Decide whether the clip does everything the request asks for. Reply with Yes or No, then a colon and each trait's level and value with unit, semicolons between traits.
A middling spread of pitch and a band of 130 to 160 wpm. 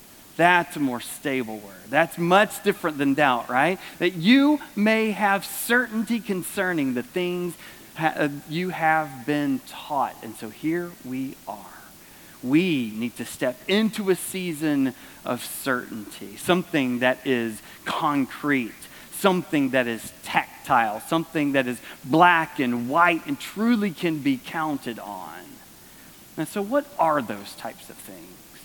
No: wide, 5.8 semitones; average, 140 wpm